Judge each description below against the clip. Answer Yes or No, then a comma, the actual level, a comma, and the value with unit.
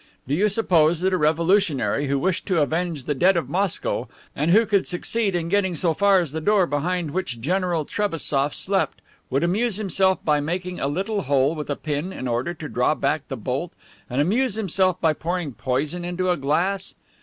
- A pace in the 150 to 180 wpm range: No, average, 200 wpm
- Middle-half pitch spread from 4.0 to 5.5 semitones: Yes, average, 4.3 semitones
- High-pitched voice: No, medium, 175 Hz